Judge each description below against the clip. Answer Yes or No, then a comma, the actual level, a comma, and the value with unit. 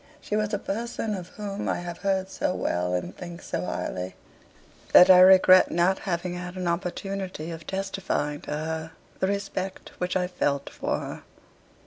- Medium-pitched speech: Yes, medium, 180 Hz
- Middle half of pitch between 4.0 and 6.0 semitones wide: No, narrow, 2.4 semitones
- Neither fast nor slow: Yes, average, 170 wpm